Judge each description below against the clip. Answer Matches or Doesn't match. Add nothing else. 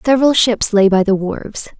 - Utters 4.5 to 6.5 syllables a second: Matches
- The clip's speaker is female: Matches